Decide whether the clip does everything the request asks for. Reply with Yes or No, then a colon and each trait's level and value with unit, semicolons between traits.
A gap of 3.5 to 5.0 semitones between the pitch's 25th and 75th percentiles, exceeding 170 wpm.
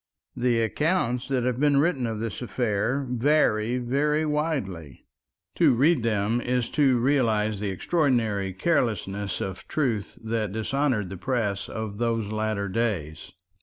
No: average, 4.4 semitones; slow, 135 wpm